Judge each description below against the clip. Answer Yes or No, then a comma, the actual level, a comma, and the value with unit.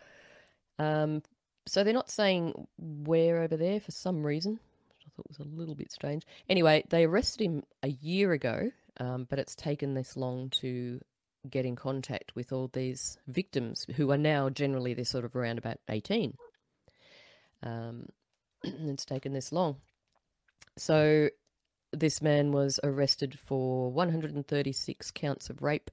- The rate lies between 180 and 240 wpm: No, average, 150 wpm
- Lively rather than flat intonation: No, average, 3.7 semitones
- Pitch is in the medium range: Yes, medium, 145 Hz